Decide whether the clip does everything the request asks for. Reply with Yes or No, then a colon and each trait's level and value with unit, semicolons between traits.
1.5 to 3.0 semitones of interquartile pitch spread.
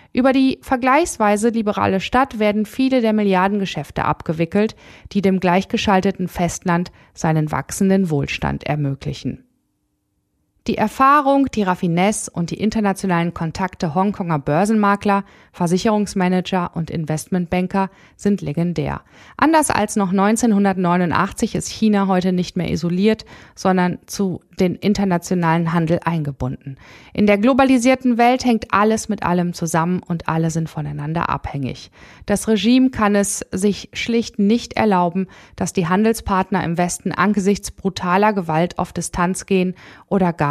No: average, 3.5 semitones